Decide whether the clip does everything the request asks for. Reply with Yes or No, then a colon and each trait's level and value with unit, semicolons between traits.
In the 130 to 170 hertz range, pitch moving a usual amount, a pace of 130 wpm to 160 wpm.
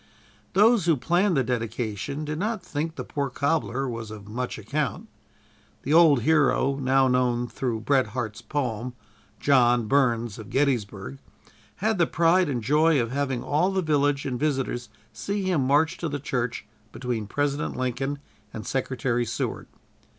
Yes: low, 135 Hz; average, 4.0 semitones; average, 155 wpm